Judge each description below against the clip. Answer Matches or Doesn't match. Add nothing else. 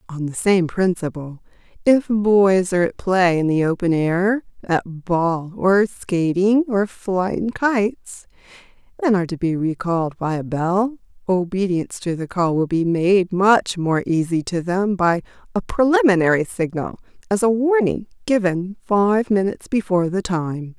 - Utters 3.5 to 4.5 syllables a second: Matches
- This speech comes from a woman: Matches